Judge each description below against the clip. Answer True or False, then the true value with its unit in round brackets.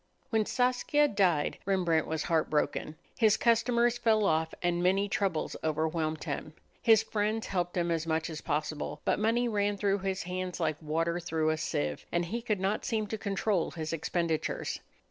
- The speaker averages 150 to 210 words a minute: True (170 wpm)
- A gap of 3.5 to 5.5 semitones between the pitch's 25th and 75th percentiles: True (5.0 semitones)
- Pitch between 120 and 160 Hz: False (180 Hz)